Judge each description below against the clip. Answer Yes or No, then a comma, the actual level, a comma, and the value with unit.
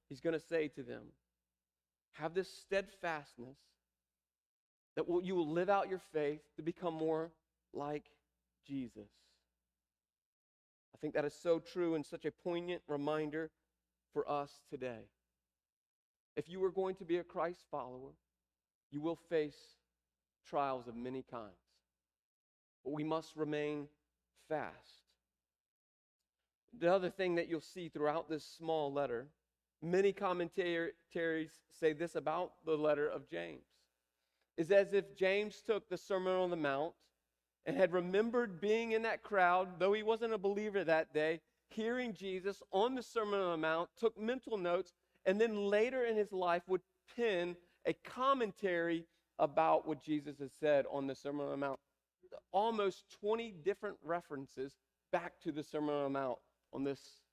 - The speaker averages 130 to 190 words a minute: Yes, average, 150 wpm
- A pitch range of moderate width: No, wide, 6.7 semitones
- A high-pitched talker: No, medium, 160 Hz